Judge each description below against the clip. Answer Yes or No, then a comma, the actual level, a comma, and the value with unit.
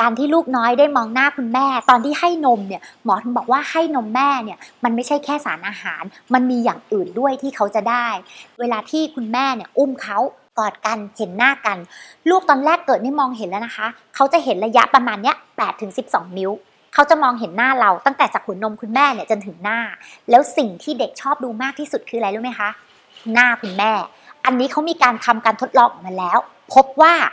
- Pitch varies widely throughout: No, average, 3.8 semitones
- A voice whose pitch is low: No, high, 245 Hz